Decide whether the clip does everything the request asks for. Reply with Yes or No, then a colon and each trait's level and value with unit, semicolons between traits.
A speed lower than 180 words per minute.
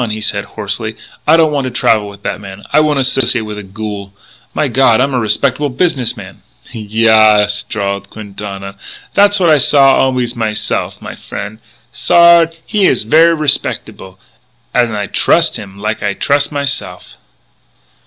Yes: average, 165 wpm